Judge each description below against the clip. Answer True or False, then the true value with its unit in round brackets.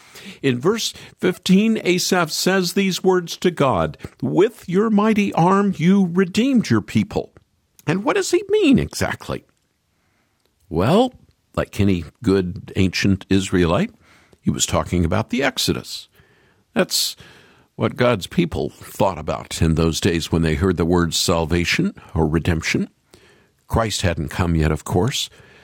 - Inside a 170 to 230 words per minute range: False (135 wpm)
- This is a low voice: True (110 Hz)